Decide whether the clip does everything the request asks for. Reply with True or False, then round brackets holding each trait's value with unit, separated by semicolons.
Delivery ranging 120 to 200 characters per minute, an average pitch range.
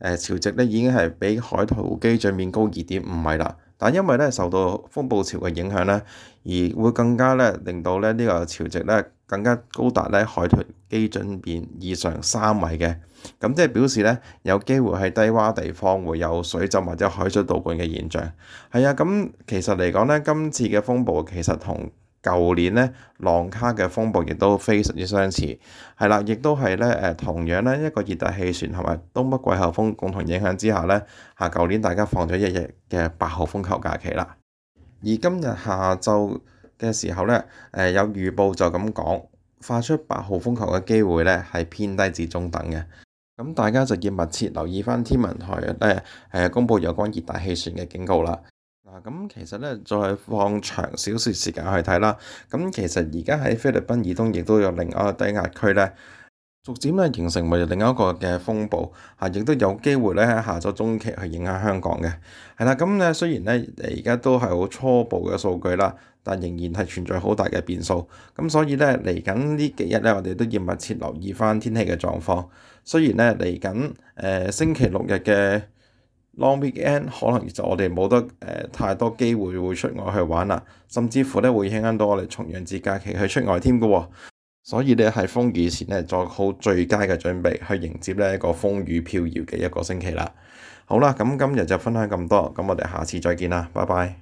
False (290 characters per minute; 4.5 semitones)